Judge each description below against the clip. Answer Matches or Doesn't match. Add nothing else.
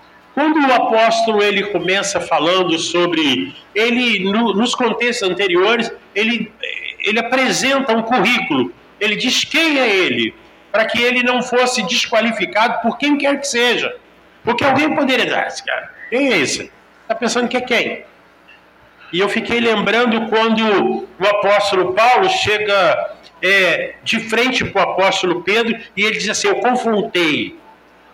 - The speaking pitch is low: Doesn't match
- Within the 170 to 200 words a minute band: Doesn't match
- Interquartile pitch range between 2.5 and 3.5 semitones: Doesn't match